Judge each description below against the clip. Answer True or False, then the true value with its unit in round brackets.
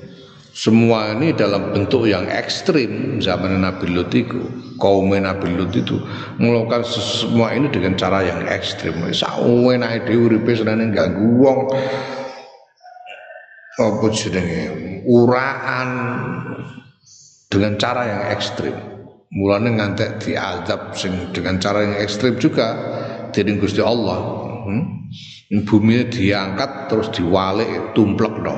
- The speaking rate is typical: True (100 wpm)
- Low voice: True (110 Hz)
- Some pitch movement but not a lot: True (3.9 semitones)